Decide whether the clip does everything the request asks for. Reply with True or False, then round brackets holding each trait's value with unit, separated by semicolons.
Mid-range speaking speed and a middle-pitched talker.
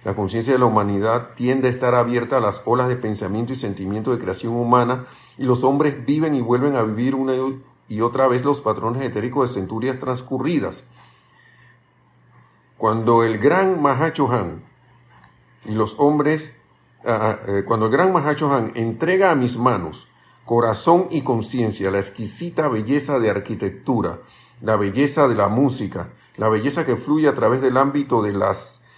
False (155 wpm; 120 Hz)